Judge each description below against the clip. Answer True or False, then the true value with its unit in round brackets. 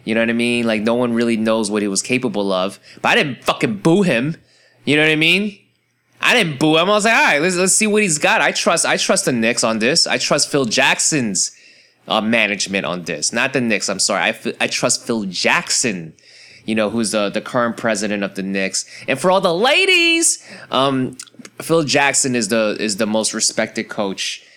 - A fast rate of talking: True (225 wpm)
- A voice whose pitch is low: True (125 Hz)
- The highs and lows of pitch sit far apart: True (7.3 semitones)